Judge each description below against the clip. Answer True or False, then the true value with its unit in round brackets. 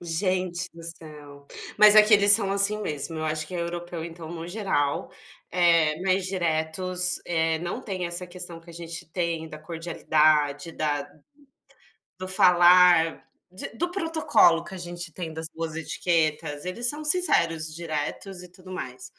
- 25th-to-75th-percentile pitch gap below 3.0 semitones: True (2.5 semitones)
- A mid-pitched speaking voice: True (170 Hz)